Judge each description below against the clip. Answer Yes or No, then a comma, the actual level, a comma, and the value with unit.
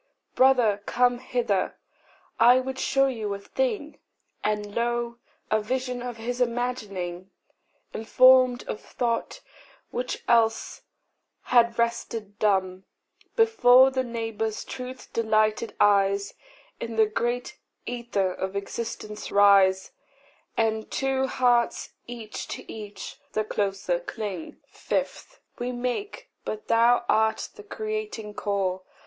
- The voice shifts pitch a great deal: No, average, 3.1 semitones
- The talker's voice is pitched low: No, high, 230 Hz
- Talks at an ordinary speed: No, slow, 115 wpm